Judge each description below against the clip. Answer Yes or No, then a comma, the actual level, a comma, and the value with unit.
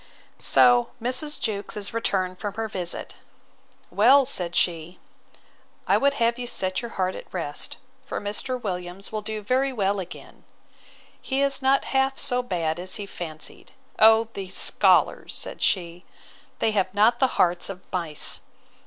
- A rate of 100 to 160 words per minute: Yes, average, 155 wpm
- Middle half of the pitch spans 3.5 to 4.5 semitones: No, average, 5.1 semitones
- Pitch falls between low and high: No, high, 205 Hz